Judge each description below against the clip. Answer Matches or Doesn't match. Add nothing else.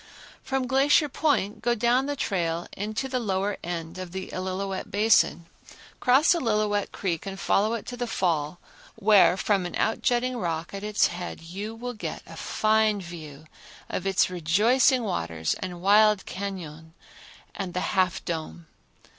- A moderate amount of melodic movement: Matches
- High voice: Matches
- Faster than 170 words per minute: Doesn't match